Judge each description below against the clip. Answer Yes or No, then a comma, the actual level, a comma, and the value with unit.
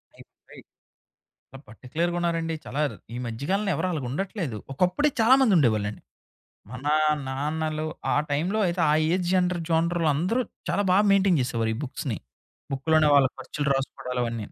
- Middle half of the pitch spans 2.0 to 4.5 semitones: No, wide, 5.4 semitones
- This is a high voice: No, medium, 155 Hz